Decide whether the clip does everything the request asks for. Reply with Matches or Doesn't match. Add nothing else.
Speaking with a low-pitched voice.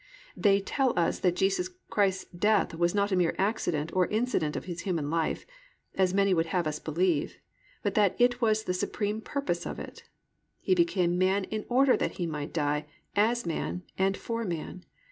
Doesn't match